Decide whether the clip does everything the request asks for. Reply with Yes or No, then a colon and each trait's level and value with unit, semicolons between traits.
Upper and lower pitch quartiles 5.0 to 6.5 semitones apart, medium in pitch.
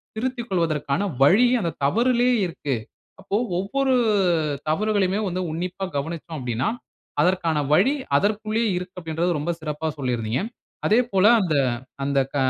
Yes: wide, 5.5 semitones; medium, 180 Hz